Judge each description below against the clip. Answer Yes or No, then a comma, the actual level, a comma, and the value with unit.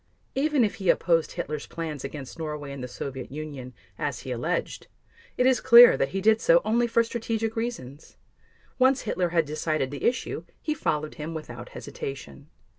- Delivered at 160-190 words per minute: Yes, average, 175 wpm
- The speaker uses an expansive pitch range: Yes, wide, 8.2 semitones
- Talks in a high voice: No, medium, 160 Hz